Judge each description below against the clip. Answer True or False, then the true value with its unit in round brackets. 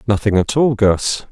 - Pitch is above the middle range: False (110 Hz)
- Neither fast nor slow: True (185 wpm)